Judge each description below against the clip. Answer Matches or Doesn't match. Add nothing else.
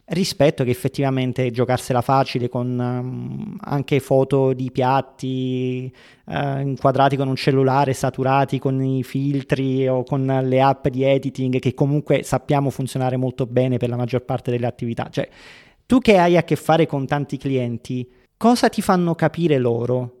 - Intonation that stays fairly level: Matches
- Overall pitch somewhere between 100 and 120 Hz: Doesn't match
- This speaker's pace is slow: Doesn't match